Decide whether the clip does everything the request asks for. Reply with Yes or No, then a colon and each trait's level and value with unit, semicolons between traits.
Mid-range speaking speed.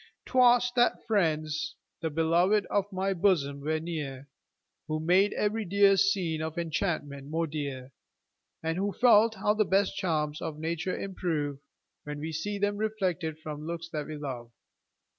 Yes: average, 155 wpm